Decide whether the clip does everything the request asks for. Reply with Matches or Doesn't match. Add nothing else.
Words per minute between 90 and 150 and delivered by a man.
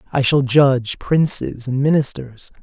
Matches